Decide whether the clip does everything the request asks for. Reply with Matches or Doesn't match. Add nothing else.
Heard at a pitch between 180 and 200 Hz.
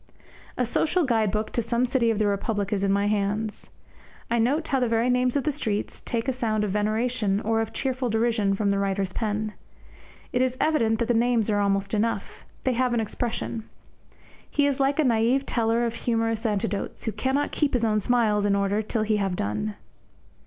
Doesn't match